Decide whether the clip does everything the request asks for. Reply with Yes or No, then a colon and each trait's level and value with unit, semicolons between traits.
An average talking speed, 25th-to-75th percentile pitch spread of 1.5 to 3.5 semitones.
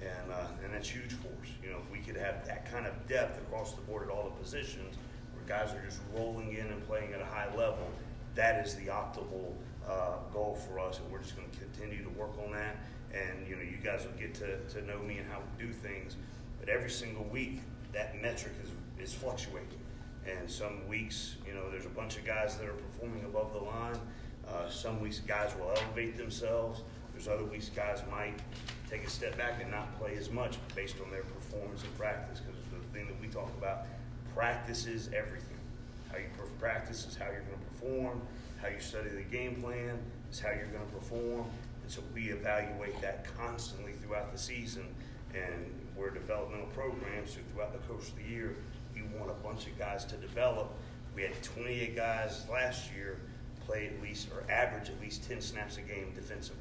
No: fast, 210 wpm; narrow, 2.6 semitones